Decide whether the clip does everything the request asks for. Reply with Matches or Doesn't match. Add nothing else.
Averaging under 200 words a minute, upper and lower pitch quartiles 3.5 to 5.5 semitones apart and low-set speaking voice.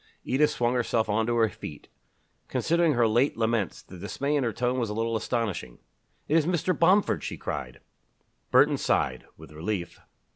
Matches